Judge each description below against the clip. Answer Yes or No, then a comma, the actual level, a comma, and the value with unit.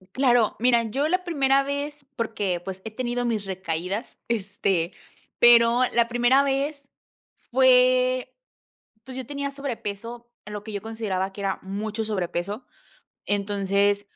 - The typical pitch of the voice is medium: No, high, 230 Hz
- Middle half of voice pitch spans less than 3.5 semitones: No, average, 4.2 semitones